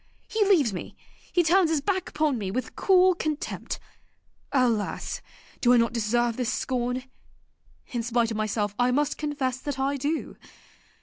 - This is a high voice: Yes, very high, 255 Hz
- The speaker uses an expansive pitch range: No, average, 4.5 semitones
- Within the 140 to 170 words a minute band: Yes, average, 160 wpm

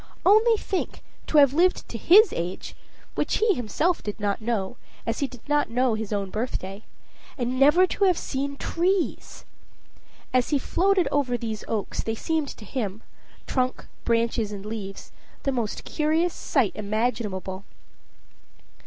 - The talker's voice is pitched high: Yes, very high, 250 Hz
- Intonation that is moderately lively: No, wide, 6.7 semitones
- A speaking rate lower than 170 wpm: Yes, average, 150 wpm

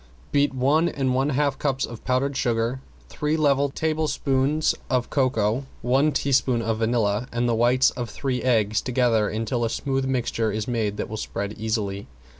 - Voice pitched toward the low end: Yes, low, 125 Hz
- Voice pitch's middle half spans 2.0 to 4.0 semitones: Yes, average, 3.3 semitones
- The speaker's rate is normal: Yes, average, 170 wpm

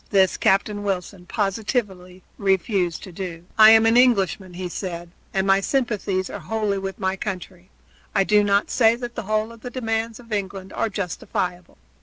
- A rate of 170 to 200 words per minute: Yes, average, 175 wpm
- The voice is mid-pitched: No, high, 195 Hz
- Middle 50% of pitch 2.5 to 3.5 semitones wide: Yes, average, 3.0 semitones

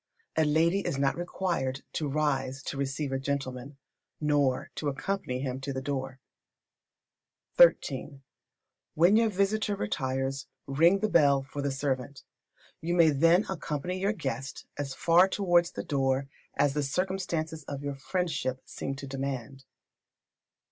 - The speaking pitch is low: No, medium, 145 Hz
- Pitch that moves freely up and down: No, average, 4.2 semitones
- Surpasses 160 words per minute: No, average, 140 wpm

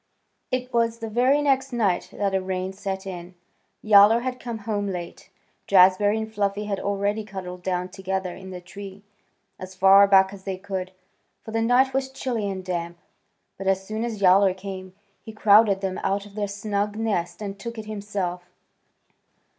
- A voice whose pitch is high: Yes, high, 200 Hz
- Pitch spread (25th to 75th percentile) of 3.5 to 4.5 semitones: No, narrow, 2.5 semitones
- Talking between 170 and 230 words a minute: Yes, average, 180 wpm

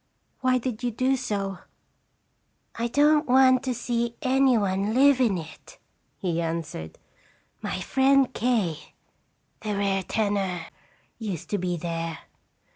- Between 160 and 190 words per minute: No, average, 140 wpm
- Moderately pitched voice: No, high, 220 Hz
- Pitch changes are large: Yes, wide, 5.8 semitones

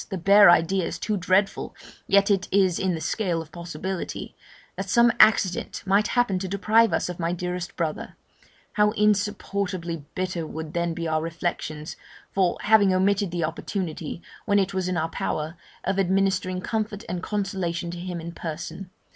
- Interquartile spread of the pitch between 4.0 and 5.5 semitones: No, average, 2.8 semitones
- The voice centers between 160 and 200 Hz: Yes, medium, 185 Hz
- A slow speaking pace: No, average, 170 wpm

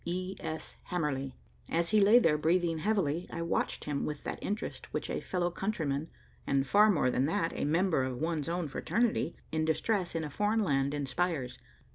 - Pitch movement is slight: No, average, 4.1 semitones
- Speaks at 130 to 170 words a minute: No, average, 185 wpm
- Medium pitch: Yes, medium, 165 Hz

